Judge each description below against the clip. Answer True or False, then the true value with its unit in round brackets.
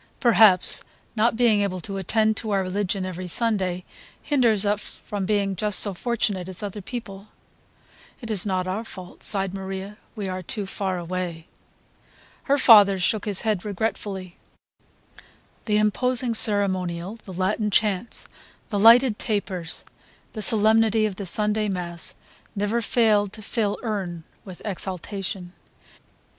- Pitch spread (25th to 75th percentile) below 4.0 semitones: True (2.7 semitones)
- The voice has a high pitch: True (205 Hz)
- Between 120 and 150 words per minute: True (140 wpm)